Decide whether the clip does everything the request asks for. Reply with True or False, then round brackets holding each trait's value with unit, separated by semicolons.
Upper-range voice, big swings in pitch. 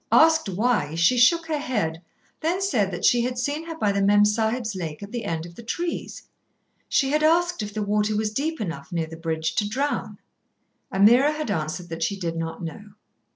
True (210 Hz; 8.0 semitones)